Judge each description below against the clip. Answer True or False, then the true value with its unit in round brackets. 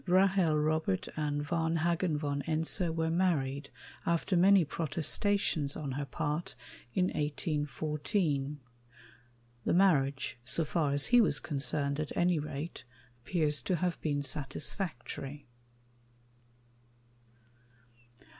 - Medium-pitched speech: True (155 Hz)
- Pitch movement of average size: True (3.2 semitones)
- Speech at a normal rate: False (105 wpm)